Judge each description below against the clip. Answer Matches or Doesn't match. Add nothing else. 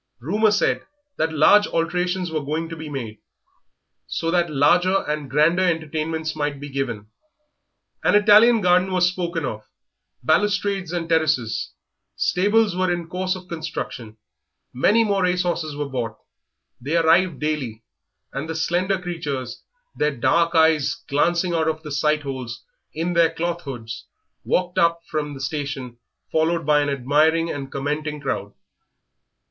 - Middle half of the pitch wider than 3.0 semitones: Matches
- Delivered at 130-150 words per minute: Matches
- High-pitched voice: Doesn't match